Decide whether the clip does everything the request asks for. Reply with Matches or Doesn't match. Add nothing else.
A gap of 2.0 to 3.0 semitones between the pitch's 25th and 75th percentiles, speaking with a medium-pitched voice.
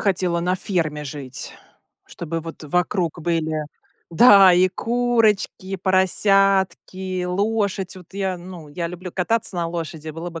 Matches